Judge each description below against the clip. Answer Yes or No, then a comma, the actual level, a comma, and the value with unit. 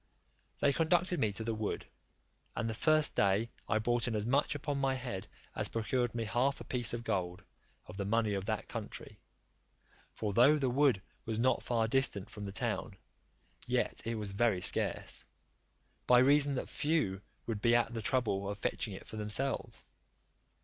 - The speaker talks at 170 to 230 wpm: Yes, average, 180 wpm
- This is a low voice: Yes, low, 115 Hz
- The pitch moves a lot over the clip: No, average, 4.0 semitones